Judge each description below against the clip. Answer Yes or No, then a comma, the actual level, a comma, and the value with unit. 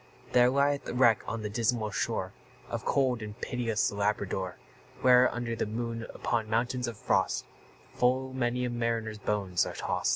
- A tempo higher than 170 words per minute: No, average, 165 wpm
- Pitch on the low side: Yes, low, 115 Hz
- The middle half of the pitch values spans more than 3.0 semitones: No, narrow, 2.5 semitones